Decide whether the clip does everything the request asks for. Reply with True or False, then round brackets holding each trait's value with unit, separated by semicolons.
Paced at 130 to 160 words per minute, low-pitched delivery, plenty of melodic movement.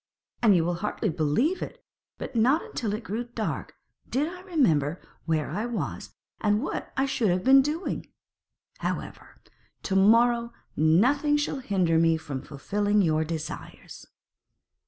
False (145 wpm; 210 Hz; 7.8 semitones)